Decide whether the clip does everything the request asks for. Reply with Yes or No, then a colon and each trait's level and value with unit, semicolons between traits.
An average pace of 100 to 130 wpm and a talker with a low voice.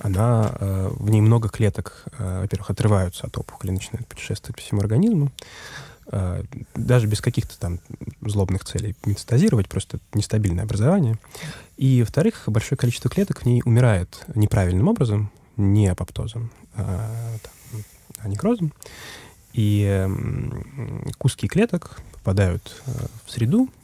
Yes: slow, 110 wpm; low, 110 Hz